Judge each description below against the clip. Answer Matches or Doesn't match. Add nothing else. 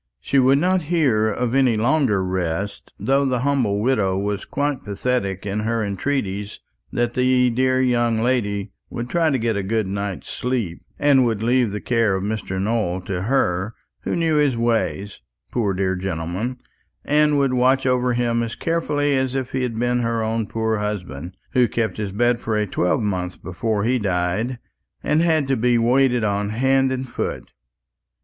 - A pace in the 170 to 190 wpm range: Matches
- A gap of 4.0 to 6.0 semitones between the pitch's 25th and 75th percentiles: Matches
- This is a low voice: Matches